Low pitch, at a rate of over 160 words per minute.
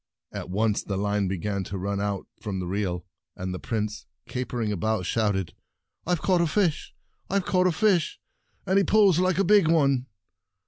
Yes: low, 110 Hz; average, 185 wpm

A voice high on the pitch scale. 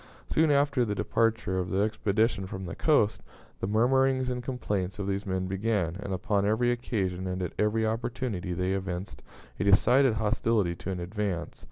No: low, 105 Hz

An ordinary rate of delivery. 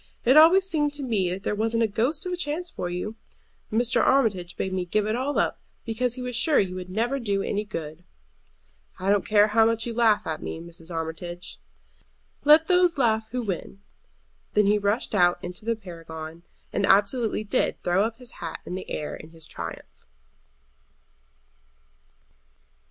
Yes: average, 180 wpm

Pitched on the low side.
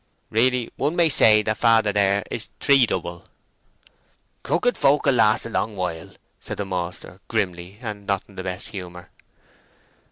Yes: low, 105 Hz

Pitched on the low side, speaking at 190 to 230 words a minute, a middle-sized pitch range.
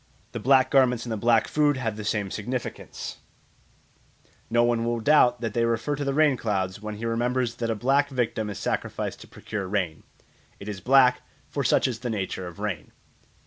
Yes: low, 115 Hz; average, 195 wpm; average, 3.4 semitones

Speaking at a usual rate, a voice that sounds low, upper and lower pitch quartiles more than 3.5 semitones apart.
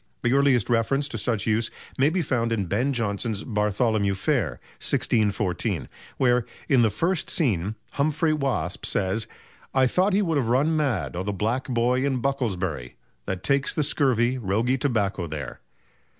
Yes: average, 160 wpm; low, 120 Hz; average, 5.2 semitones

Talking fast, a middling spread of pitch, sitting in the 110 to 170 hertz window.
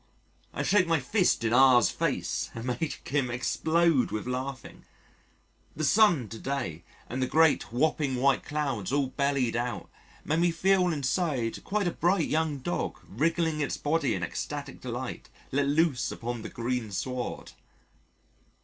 No: average, 155 wpm; average, 4.7 semitones; medium, 140 Hz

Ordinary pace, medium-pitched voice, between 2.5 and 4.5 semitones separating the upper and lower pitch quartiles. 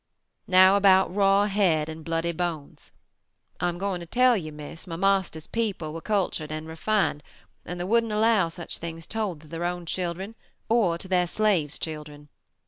Yes: average, 175 wpm; medium, 175 Hz; average, 3.6 semitones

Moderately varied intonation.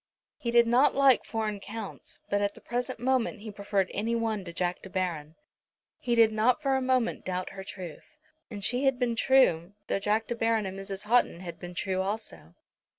Yes: average, 4.0 semitones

